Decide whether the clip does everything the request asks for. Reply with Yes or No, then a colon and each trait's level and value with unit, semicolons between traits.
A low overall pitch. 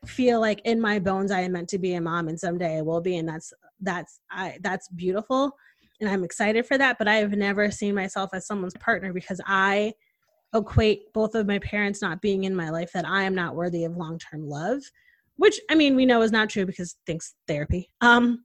No: high, 195 Hz